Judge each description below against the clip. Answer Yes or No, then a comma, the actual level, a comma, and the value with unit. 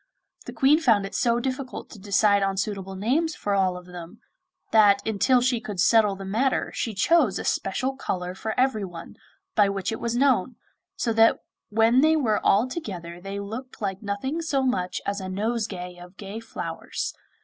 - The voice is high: Yes, high, 210 Hz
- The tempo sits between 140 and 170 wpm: No, average, 180 wpm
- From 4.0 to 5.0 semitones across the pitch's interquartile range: Yes, average, 4.4 semitones